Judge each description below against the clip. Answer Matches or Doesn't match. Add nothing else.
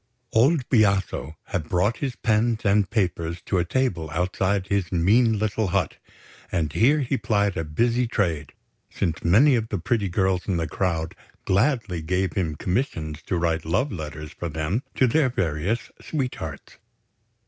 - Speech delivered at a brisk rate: Doesn't match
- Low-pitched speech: Matches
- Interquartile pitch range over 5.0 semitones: Matches